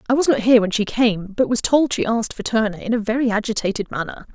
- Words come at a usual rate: No, fast, 265 wpm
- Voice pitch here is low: No, high, 225 Hz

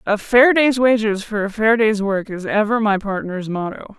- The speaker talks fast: Yes, fast, 210 wpm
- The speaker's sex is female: Yes, female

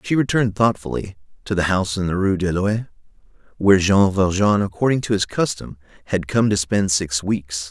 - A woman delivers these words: No, male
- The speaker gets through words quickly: No, average, 185 wpm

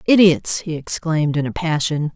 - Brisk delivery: No, average, 165 wpm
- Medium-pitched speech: Yes, medium, 160 Hz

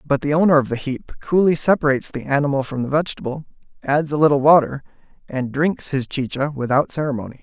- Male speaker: Yes, male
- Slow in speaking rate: No, average, 185 wpm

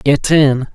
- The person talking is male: Yes, male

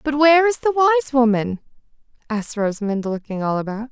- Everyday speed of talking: Yes, average, 170 wpm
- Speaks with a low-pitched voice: No, very high, 250 Hz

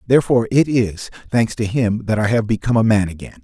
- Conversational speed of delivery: No, fast, 225 wpm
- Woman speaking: No, male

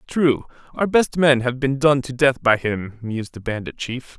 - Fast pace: Yes, fast, 215 wpm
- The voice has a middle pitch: No, low, 130 Hz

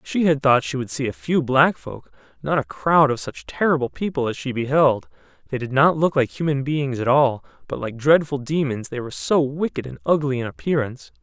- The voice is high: No, low, 135 Hz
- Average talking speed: No, fast, 220 wpm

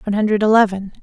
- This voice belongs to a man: No, female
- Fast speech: No, average, 175 wpm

